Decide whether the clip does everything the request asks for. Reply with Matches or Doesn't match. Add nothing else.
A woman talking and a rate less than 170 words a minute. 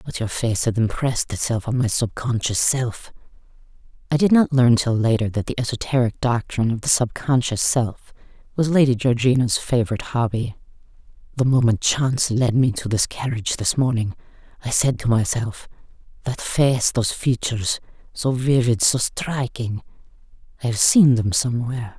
Matches